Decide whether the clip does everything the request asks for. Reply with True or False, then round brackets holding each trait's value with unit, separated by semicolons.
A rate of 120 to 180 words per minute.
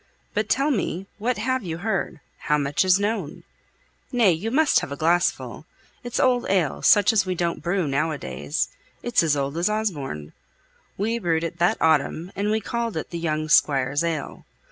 False (190 wpm)